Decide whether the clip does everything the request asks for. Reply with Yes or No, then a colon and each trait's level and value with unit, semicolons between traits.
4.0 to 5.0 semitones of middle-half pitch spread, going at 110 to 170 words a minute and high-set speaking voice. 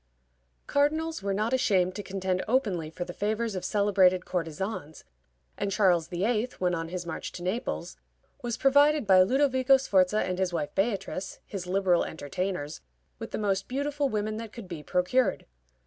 Yes: average, 4.7 semitones; average, 165 wpm; high, 195 Hz